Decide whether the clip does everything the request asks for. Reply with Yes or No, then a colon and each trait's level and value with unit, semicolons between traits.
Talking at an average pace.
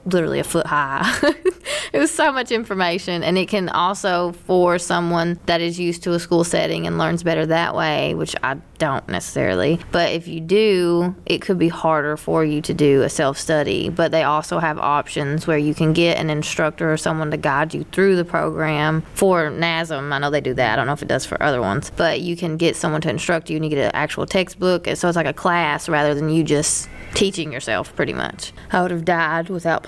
No: fast, 225 wpm